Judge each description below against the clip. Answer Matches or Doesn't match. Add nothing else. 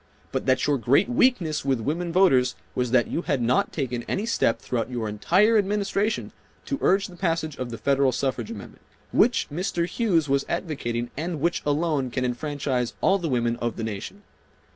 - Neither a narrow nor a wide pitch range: Doesn't match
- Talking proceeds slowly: Doesn't match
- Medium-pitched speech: Matches